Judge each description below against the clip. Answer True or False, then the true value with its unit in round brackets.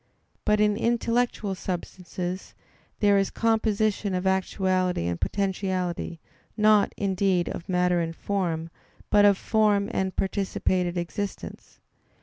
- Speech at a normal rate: False (115 wpm)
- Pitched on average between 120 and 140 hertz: False (190 Hz)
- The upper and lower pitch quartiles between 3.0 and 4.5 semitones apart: False (2.4 semitones)